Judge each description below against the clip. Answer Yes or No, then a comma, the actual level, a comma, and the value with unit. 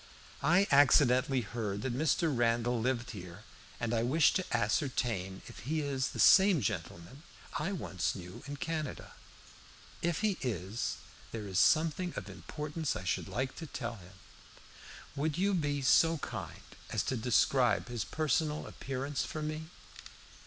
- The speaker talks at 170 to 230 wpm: No, average, 150 wpm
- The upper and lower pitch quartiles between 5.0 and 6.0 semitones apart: Yes, wide, 5.5 semitones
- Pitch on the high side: No, low, 130 Hz